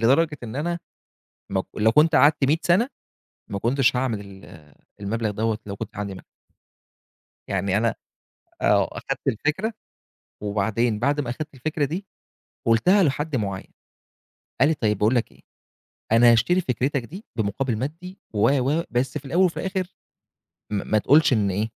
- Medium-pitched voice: No, low, 125 Hz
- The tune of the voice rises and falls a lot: Yes, wide, 6.3 semitones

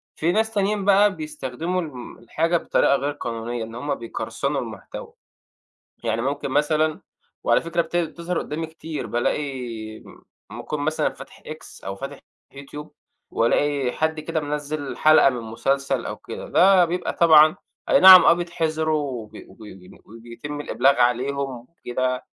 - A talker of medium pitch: Yes, medium, 145 Hz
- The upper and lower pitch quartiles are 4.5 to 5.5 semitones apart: Yes, average, 4.8 semitones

